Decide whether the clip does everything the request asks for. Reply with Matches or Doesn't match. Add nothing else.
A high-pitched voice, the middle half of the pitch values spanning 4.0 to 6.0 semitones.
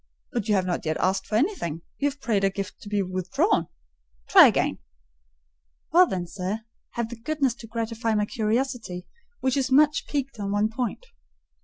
Matches